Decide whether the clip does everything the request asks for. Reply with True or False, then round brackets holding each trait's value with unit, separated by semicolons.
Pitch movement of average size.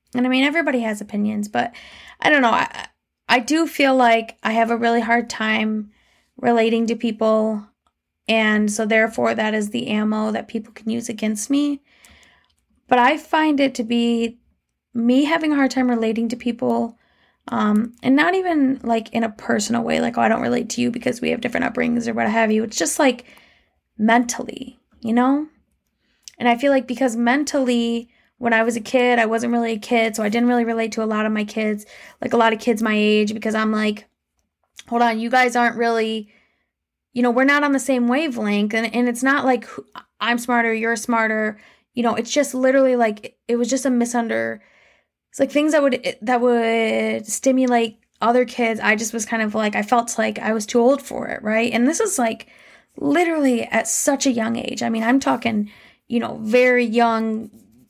False (2.1 semitones)